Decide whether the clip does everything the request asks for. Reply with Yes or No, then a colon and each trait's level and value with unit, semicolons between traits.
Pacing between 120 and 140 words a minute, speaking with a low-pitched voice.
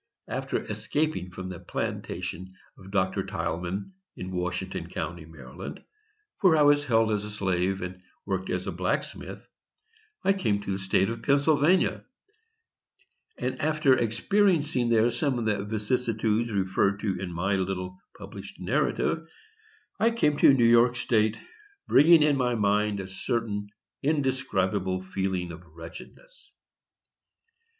Yes: slow, 135 wpm; low, 105 Hz